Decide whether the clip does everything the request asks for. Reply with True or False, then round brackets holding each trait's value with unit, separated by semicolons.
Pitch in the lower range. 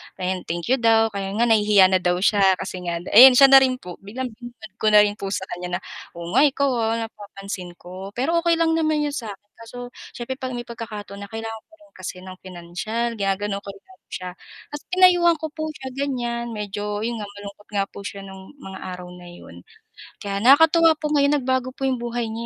False (220 Hz)